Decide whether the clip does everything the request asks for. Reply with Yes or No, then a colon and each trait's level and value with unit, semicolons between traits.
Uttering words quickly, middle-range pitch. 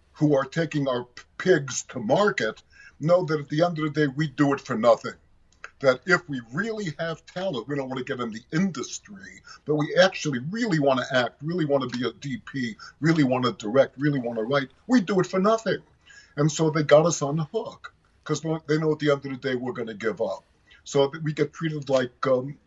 Yes: fast, 235 wpm; medium, 150 Hz